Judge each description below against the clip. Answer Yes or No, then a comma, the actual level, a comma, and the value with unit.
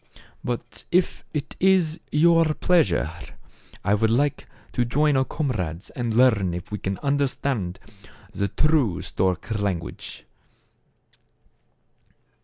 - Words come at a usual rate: No, slow, 115 wpm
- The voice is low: Yes, low, 125 Hz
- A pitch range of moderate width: No, wide, 7.2 semitones